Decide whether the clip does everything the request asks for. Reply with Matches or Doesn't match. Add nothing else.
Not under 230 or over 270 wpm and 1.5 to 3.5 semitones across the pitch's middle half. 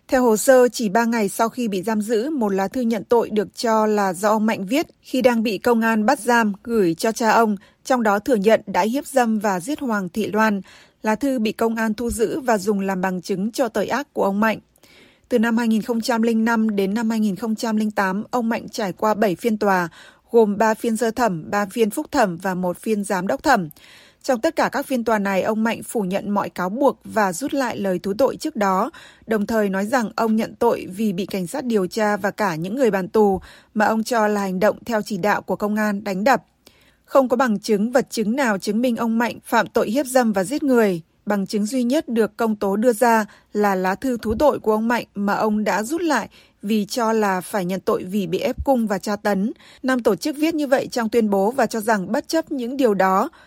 Matches